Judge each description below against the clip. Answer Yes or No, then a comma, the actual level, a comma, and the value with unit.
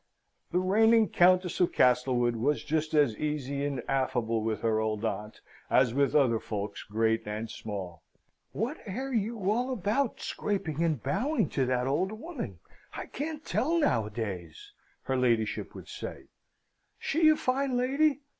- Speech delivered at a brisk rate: No, average, 150 wpm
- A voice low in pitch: No, medium, 145 Hz